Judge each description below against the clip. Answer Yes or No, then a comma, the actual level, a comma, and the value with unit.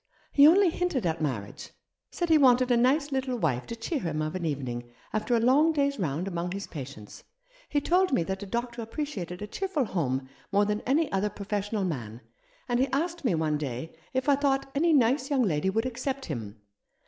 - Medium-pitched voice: No, high, 225 Hz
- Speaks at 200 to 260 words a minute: Yes, fast, 205 wpm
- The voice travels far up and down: Yes, wide, 9.0 semitones